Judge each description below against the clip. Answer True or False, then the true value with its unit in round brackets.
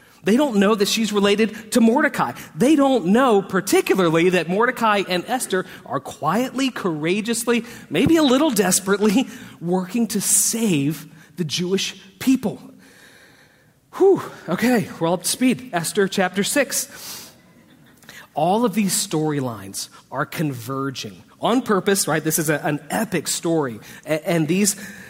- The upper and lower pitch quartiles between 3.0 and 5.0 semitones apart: False (5.6 semitones)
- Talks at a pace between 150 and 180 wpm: False (135 wpm)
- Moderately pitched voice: False (200 Hz)